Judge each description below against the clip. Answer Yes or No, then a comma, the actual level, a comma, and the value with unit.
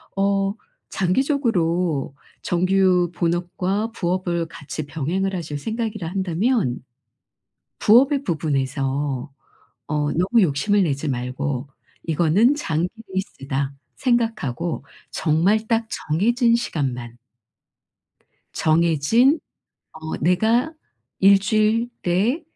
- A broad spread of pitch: Yes, wide, 6.1 semitones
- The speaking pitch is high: No, medium, 180 Hz